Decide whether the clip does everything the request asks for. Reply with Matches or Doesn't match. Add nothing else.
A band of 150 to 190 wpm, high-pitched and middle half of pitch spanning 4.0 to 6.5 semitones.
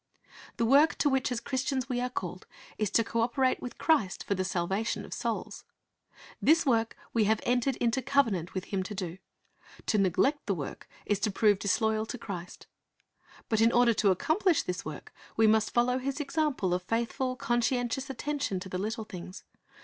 Matches